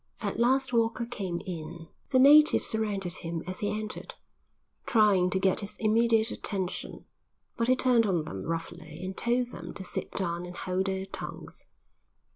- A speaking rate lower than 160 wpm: No, average, 165 wpm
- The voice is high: Yes, high, 195 Hz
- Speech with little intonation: No, average, 4.6 semitones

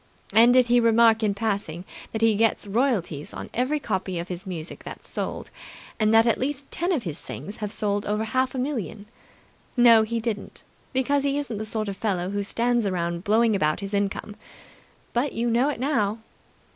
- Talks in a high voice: Yes, high, 220 Hz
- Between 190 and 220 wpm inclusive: Yes, average, 195 wpm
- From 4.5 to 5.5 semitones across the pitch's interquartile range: No, average, 3.4 semitones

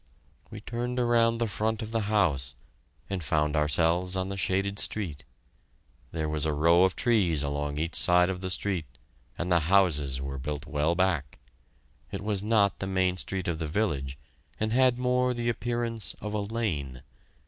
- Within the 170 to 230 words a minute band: Yes, average, 175 wpm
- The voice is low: Yes, very low, 95 Hz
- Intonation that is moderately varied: No, wide, 6.0 semitones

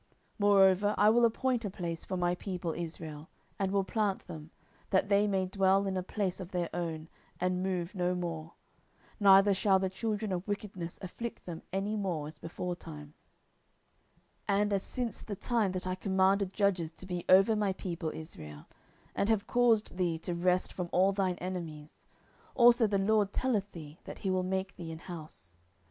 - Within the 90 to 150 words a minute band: No, average, 185 wpm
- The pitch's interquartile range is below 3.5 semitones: Yes, average, 2.7 semitones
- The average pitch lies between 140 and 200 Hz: Yes, high, 190 Hz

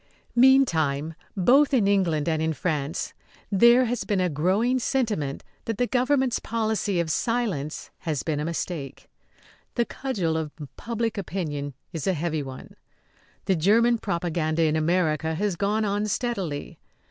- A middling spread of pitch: No, wide, 6.5 semitones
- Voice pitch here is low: No, medium, 185 Hz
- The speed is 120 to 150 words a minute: Yes, average, 145 wpm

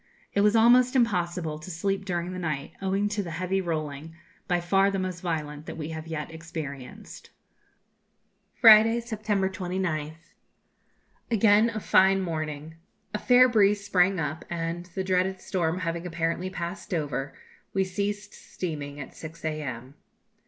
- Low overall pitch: No, medium, 180 Hz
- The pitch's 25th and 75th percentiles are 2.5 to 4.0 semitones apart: Yes, average, 3.7 semitones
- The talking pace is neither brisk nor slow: Yes, average, 145 wpm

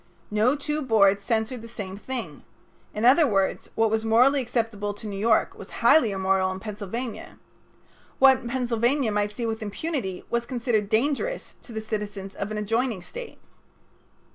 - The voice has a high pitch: Yes, high, 225 Hz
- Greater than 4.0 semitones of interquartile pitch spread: No, average, 3.3 semitones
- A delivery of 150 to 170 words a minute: Yes, average, 160 wpm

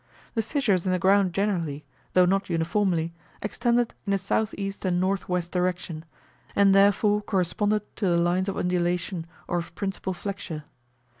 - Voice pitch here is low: No, high, 190 Hz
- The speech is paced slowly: No, average, 150 wpm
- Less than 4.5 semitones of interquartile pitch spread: Yes, narrow, 2.5 semitones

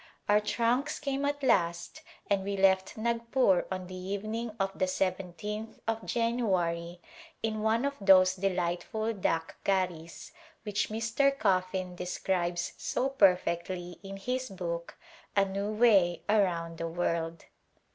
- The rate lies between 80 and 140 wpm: Yes, slow, 135 wpm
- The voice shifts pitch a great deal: No, average, 4.0 semitones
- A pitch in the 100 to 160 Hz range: No, high, 195 Hz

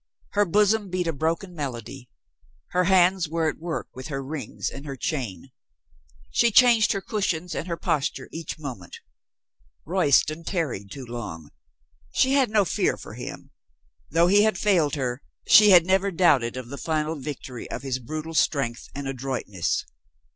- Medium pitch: Yes, medium, 155 Hz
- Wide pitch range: Yes, wide, 5.7 semitones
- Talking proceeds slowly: No, average, 160 wpm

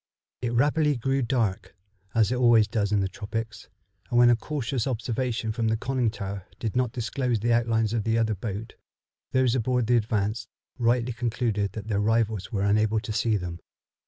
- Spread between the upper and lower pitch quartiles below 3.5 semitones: Yes, narrow, 2.4 semitones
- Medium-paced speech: Yes, average, 185 wpm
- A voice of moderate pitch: No, low, 115 Hz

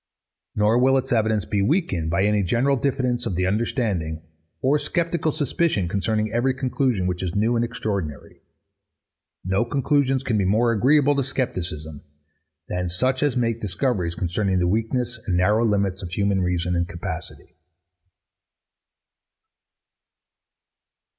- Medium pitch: No, low, 110 Hz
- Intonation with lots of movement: Yes, wide, 5.8 semitones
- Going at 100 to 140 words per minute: Yes, slow, 135 wpm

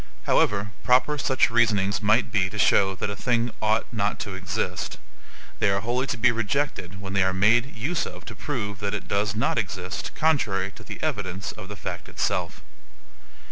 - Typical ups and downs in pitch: Yes, average, 3.4 semitones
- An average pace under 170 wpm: No, average, 185 wpm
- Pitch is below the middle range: Yes, low, 105 Hz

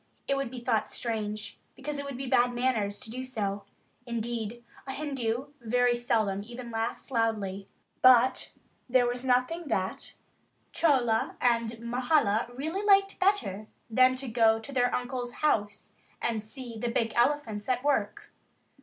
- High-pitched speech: Yes, high, 240 Hz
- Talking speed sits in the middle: Yes, average, 150 wpm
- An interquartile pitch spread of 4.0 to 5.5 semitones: No, average, 2.7 semitones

